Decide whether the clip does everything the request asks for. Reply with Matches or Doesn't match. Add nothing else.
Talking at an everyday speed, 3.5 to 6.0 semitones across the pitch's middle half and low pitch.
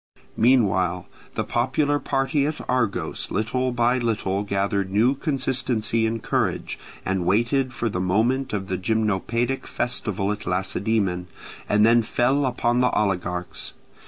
Doesn't match